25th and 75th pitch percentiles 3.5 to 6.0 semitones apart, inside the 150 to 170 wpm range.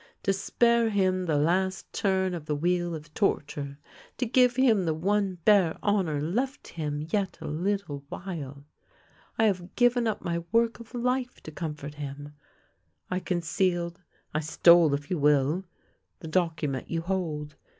Yes: average, 4.9 semitones; average, 160 wpm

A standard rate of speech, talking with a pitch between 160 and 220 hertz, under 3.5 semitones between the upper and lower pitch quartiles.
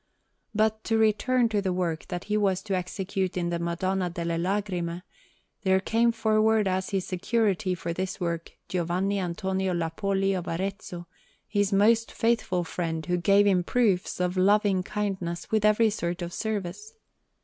Yes: average, 160 wpm; high, 190 Hz; average, 2.9 semitones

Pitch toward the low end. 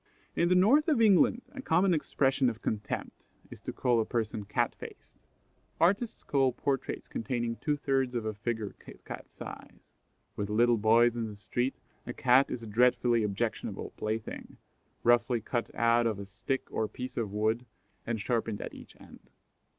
Yes: low, 120 Hz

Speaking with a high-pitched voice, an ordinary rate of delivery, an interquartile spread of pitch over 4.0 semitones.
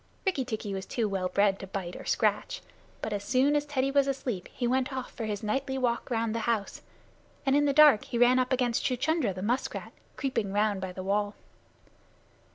No: high, 235 Hz; fast, 210 wpm; average, 4.6 semitones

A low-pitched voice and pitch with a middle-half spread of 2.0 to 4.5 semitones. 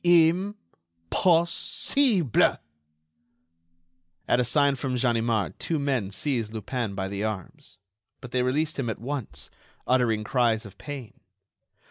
No: low, 125 Hz; average, 5.0 semitones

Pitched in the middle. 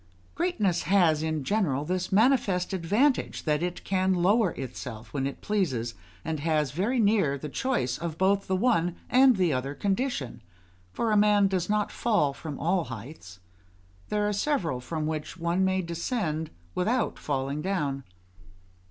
Yes: medium, 175 Hz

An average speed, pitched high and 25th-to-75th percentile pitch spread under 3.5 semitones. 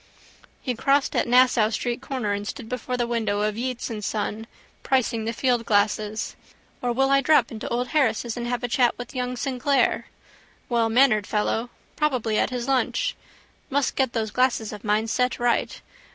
Yes: average, 175 wpm; high, 240 Hz; narrow, 2.6 semitones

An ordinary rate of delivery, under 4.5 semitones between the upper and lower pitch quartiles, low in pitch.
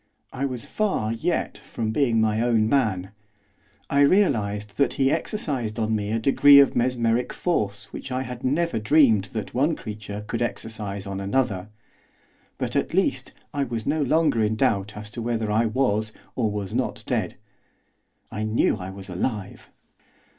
Yes: average, 165 wpm; average, 4.0 semitones; low, 115 Hz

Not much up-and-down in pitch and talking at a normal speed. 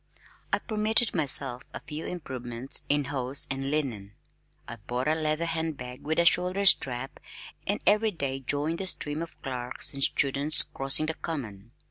No: average, 4.1 semitones; average, 165 wpm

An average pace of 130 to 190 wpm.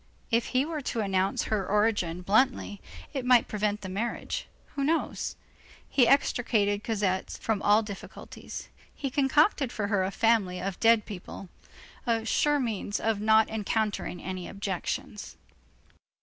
Yes: average, 140 wpm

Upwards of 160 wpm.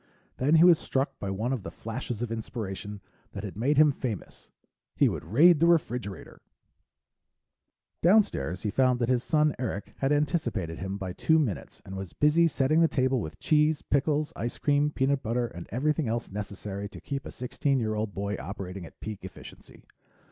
Yes: average, 185 wpm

